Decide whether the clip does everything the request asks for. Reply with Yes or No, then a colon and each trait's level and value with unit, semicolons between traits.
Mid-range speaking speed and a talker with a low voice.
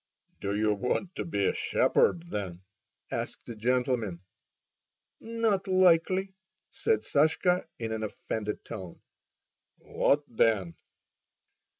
No: slow, 105 wpm; low, 120 Hz